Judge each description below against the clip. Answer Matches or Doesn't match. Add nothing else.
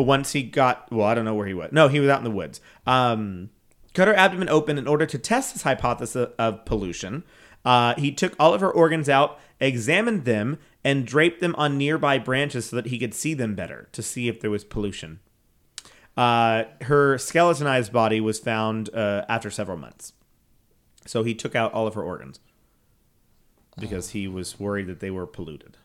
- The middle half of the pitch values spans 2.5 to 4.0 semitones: Doesn't match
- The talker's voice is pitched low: Matches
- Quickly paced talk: Doesn't match